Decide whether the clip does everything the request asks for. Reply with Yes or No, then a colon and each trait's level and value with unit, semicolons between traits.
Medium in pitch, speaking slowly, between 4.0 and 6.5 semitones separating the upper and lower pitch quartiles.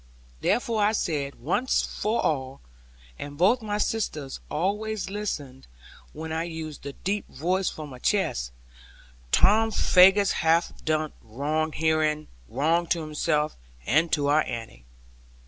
Yes: medium, 160 Hz; slow, 130 wpm; average, 5.2 semitones